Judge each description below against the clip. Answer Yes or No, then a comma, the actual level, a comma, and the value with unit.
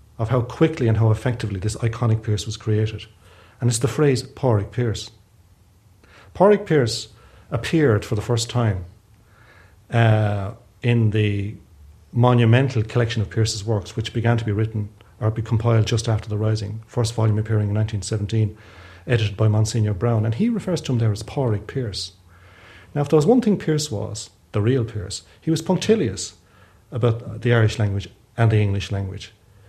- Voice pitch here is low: Yes, low, 110 Hz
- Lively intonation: No, narrow, 2.5 semitones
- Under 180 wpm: Yes, average, 170 wpm